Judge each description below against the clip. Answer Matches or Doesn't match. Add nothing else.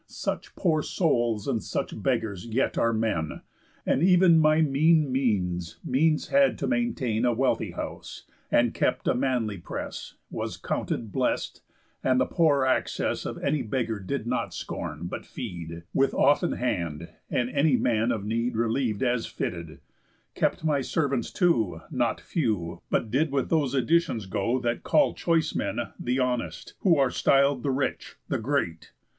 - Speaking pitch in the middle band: Doesn't match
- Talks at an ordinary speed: Matches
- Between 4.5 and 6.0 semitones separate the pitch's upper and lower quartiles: Matches